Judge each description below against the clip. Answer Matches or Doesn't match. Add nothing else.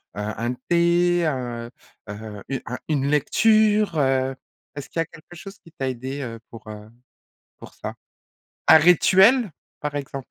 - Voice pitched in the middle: Matches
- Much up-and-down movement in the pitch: Matches